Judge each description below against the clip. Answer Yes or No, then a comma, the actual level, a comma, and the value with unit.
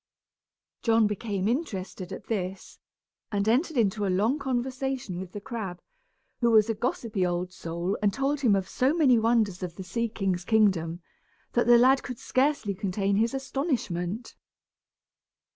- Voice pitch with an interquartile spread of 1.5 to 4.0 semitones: No, average, 4.7 semitones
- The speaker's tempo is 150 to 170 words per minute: Yes, average, 155 wpm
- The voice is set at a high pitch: Yes, high, 215 Hz